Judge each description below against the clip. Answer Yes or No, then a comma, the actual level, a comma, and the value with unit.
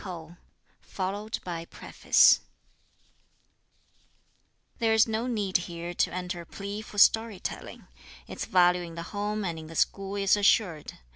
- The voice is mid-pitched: No, high, 195 Hz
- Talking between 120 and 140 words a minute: Yes, slow, 135 wpm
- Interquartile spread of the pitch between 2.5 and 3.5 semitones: Yes, average, 3.2 semitones